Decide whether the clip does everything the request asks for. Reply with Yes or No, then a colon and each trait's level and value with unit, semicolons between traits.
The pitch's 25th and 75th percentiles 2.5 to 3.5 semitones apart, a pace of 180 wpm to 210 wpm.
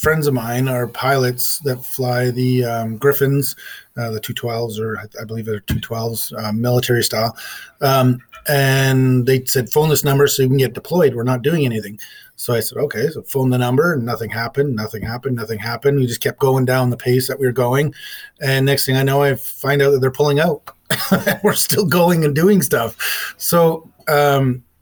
Yes: average, 2.9 semitones; average, 200 wpm